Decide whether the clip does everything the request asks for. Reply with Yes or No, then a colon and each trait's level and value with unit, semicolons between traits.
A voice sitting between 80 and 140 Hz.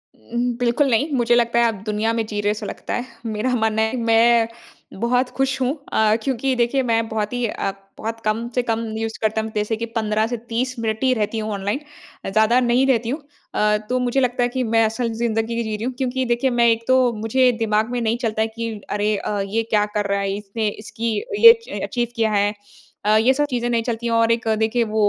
No: high, 230 Hz